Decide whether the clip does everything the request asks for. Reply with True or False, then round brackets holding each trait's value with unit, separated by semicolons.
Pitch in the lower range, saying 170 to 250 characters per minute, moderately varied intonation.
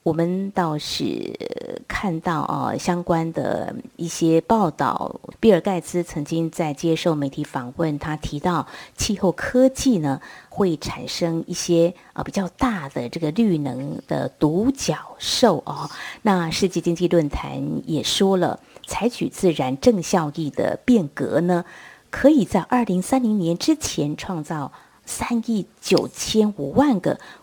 False (175 Hz; 205 characters per minute; 4.7 semitones)